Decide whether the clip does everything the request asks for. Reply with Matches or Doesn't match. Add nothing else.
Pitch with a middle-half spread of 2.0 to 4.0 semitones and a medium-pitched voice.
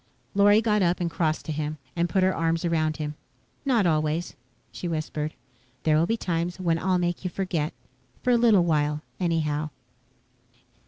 Matches